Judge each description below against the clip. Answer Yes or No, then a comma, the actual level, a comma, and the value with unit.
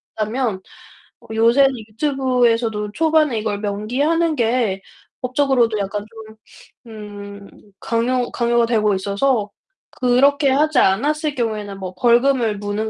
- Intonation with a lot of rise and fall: No, average, 4.0 semitones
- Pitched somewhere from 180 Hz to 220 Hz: No, high, 230 Hz